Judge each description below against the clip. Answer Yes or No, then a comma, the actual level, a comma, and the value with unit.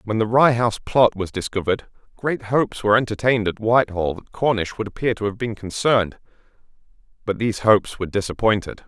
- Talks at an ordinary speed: Yes, average, 175 wpm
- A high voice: No, low, 110 Hz